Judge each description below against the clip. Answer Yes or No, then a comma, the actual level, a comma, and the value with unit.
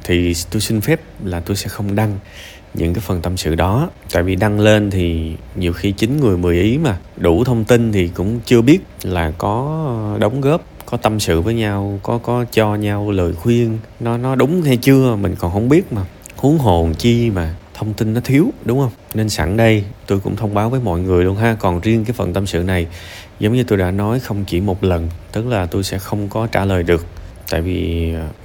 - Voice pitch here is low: Yes, low, 105 Hz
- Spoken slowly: No, average, 230 wpm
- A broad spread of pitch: No, average, 4.6 semitones